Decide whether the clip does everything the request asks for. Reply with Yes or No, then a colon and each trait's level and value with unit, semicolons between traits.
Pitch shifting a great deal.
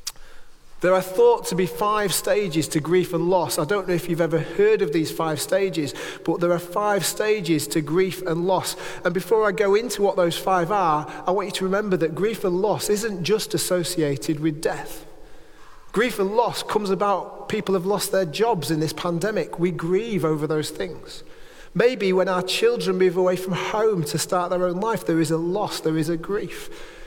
No: average, 3.5 semitones